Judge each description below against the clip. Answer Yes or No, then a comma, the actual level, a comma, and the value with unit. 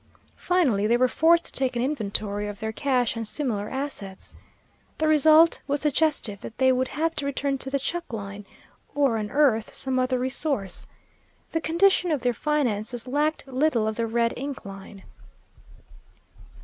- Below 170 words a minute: Yes, average, 160 wpm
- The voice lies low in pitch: No, very high, 260 Hz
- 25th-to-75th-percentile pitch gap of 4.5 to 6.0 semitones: Yes, wide, 5.4 semitones